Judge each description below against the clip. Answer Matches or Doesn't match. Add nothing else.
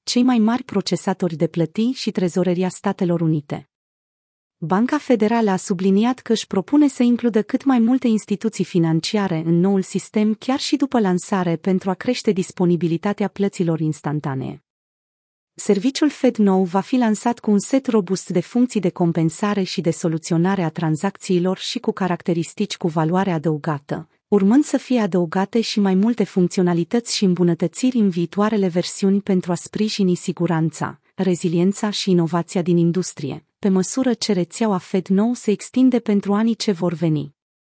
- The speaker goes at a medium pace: Matches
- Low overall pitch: Doesn't match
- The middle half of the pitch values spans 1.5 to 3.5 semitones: Doesn't match